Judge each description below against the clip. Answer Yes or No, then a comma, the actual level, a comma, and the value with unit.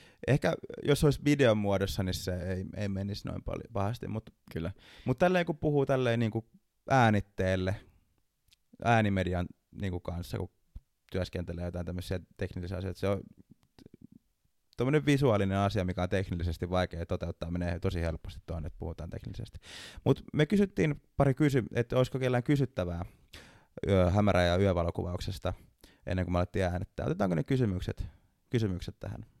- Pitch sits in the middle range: No, very low, 95 Hz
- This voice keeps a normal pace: Yes, average, 145 wpm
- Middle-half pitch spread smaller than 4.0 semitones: No, average, 4.7 semitones